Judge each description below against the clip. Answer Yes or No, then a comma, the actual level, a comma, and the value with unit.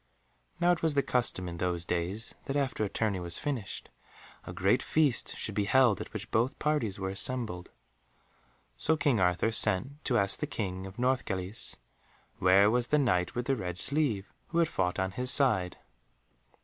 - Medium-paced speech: Yes, average, 180 wpm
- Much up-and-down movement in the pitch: Yes, wide, 6.0 semitones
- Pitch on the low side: Yes, low, 110 Hz